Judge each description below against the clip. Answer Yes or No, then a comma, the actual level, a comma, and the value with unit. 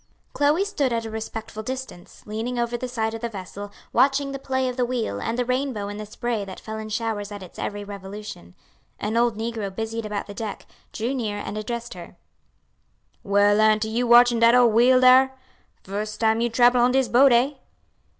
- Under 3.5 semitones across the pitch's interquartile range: Yes, average, 2.8 semitones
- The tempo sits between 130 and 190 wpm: No, average, 200 wpm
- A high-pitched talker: Yes, high, 225 Hz